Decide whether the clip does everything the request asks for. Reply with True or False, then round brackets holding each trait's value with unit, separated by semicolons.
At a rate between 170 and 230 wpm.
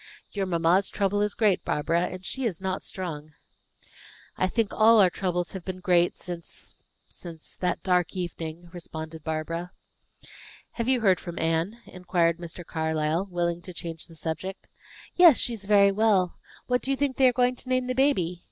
True (180 wpm)